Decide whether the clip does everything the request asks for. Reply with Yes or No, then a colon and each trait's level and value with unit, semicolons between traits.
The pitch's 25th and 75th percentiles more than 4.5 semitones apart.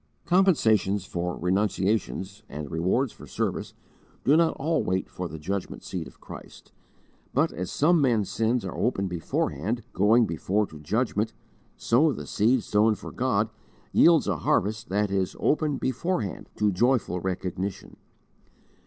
Yes: average, 4.9 semitones